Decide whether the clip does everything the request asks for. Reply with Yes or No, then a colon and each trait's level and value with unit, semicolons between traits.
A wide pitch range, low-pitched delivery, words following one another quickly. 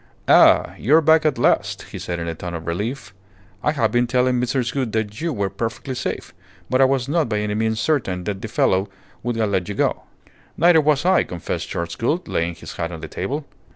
Yes: wide, 6.2 semitones; low, 115 Hz; fast, 225 wpm